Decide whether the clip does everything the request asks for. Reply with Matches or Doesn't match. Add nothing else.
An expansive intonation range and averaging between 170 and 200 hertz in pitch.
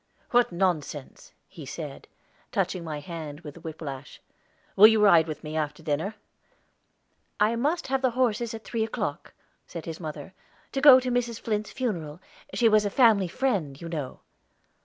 Matches